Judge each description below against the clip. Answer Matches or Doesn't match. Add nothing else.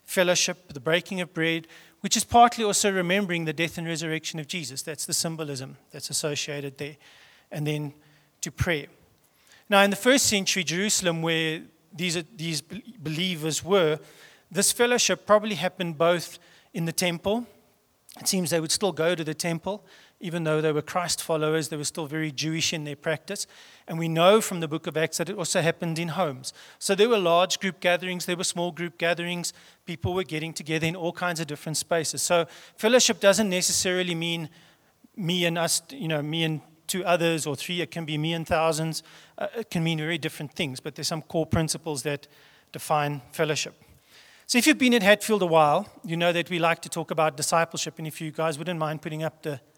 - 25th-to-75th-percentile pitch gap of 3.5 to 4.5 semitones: Doesn't match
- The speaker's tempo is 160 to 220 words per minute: Matches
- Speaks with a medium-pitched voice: Matches